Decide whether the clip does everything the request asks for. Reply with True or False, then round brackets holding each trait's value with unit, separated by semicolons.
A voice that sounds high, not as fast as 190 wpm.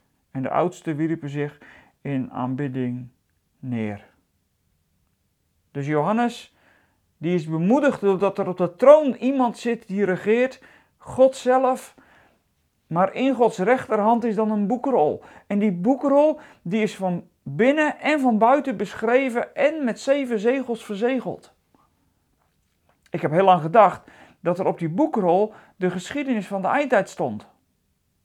True (195 Hz; 135 wpm)